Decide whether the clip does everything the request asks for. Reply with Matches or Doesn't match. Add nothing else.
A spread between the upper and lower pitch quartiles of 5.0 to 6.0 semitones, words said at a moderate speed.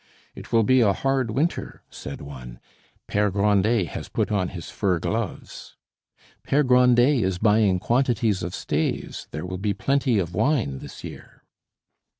Matches